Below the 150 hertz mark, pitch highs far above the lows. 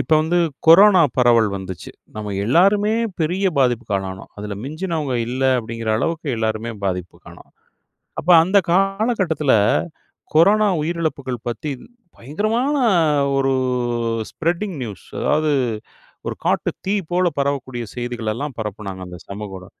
Yes: medium, 140 Hz; wide, 7.9 semitones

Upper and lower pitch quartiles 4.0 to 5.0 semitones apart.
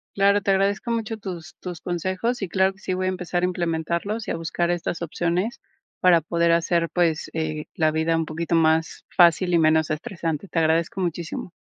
No: narrow, 2.5 semitones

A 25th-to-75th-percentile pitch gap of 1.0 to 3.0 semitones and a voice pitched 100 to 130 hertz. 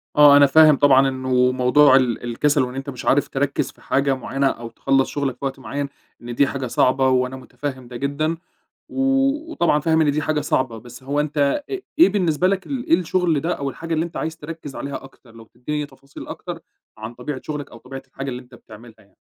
No: average, 2.7 semitones; medium, 140 Hz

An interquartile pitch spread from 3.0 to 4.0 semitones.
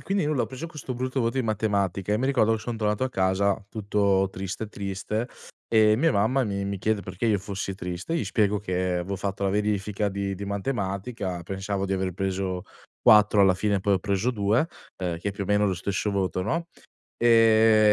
No: narrow, 2.5 semitones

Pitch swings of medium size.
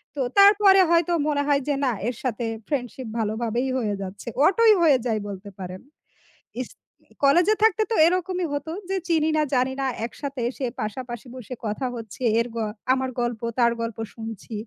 No: wide, 6.3 semitones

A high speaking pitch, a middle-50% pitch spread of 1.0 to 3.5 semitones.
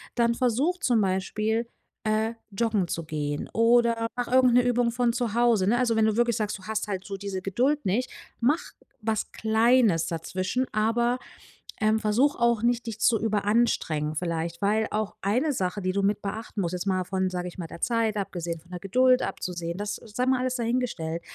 No: high, 220 Hz; average, 4.1 semitones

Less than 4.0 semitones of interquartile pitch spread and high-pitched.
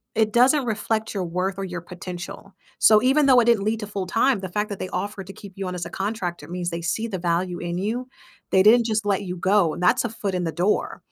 Yes: average, 3.5 semitones; high, 195 Hz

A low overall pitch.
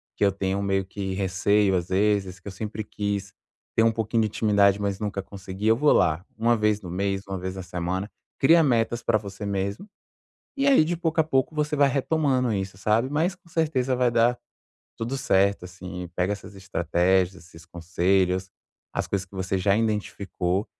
Yes: low, 100 Hz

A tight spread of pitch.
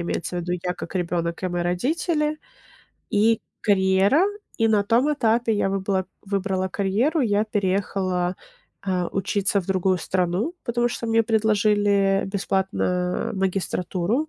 No: average, 3.2 semitones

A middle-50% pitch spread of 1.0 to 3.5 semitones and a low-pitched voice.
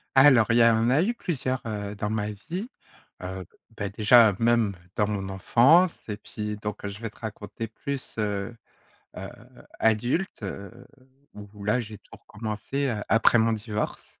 Yes: average, 2.7 semitones; low, 110 Hz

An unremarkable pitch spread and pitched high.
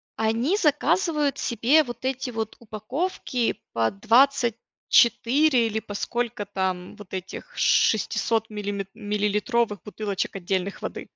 Yes: average, 4.1 semitones; high, 225 Hz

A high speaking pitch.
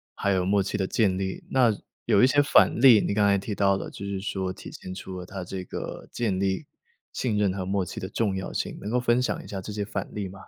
No: low, 100 Hz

